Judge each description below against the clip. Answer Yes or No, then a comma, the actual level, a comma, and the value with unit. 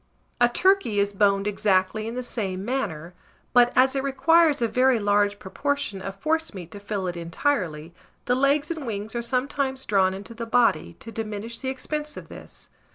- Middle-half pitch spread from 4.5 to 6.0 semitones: Yes, average, 5.1 semitones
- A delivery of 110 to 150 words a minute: No, average, 180 wpm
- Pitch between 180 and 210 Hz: No, high, 230 Hz